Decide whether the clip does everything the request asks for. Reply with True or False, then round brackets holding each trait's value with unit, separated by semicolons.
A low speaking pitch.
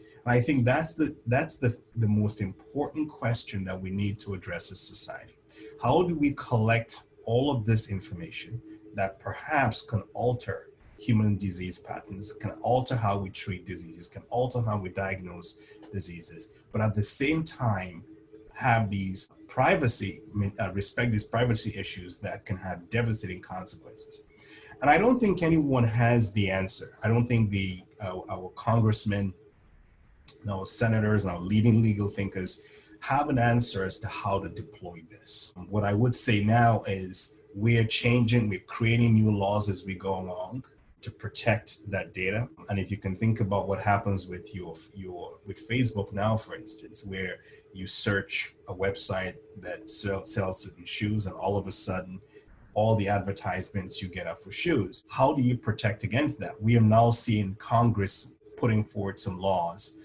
True (105 Hz)